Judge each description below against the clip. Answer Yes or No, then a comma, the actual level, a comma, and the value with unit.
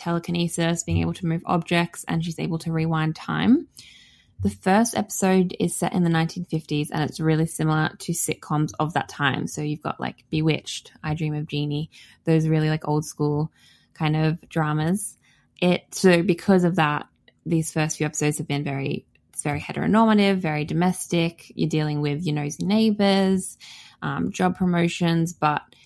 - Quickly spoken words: No, average, 170 wpm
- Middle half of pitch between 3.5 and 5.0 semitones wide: No, average, 2.8 semitones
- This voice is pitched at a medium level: Yes, medium, 160 Hz